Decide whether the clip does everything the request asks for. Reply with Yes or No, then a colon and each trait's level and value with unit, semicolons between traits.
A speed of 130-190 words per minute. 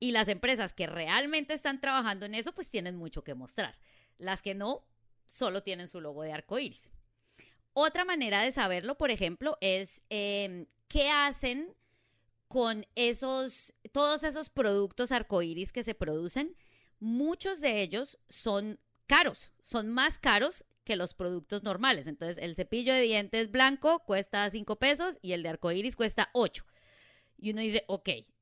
Yes: average, 160 wpm